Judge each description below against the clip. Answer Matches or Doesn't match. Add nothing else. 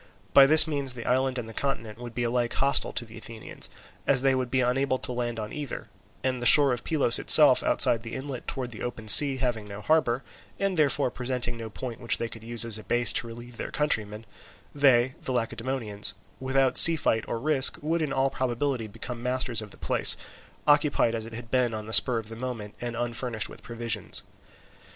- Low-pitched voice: Matches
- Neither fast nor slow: Doesn't match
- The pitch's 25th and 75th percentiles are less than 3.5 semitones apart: Matches